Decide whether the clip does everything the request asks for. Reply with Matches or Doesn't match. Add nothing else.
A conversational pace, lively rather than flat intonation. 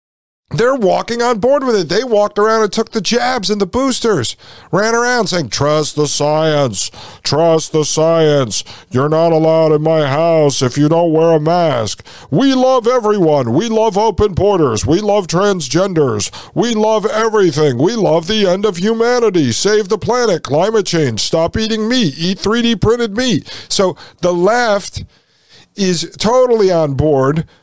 Matches